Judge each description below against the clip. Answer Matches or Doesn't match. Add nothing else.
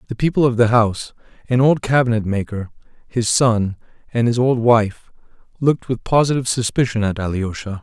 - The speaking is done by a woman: Doesn't match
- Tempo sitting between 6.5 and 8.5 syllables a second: Doesn't match